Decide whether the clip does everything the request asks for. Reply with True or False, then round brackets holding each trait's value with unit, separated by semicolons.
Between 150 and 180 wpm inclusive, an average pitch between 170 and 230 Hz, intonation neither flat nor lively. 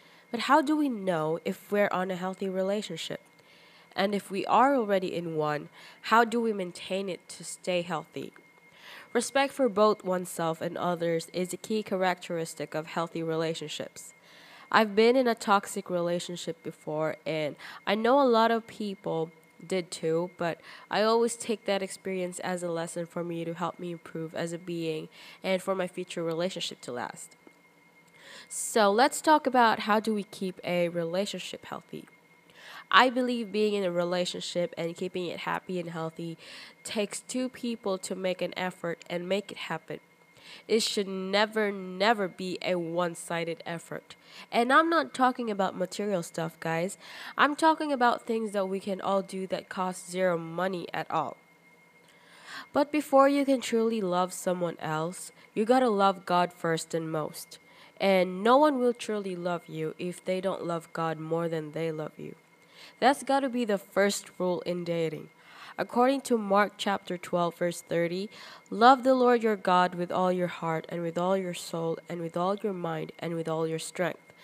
True (175 wpm; 185 Hz; 4.0 semitones)